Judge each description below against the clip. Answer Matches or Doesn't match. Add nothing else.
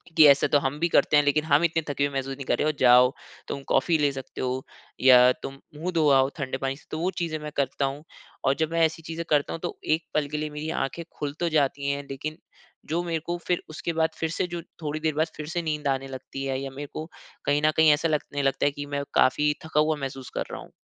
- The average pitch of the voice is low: Doesn't match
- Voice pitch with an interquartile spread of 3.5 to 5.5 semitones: Doesn't match